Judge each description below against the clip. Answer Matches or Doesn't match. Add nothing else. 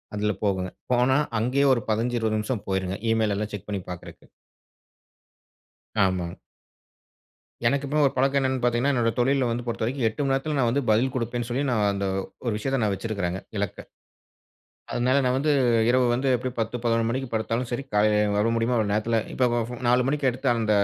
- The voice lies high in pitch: Doesn't match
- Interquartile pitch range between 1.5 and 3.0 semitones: Doesn't match